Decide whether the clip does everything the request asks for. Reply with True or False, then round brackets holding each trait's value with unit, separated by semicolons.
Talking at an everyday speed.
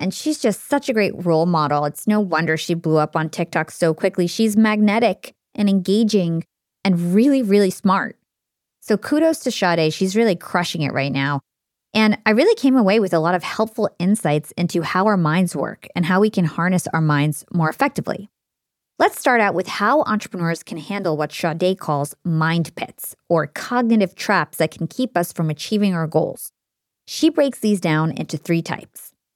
True (190 wpm)